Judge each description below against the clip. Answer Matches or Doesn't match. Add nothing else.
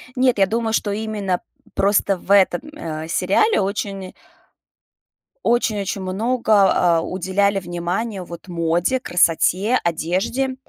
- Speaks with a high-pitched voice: Matches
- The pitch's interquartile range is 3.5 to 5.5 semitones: Matches